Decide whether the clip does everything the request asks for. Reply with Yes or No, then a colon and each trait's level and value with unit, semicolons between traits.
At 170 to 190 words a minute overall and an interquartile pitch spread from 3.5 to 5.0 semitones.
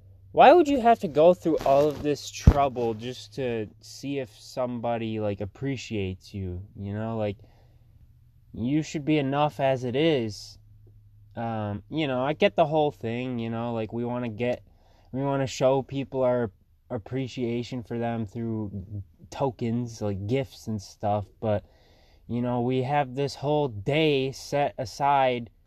No: average, 160 wpm; average, 4.6 semitones